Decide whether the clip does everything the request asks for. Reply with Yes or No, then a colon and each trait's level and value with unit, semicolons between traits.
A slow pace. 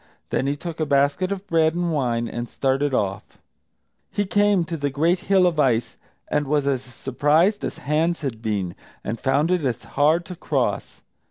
No: average, 185 wpm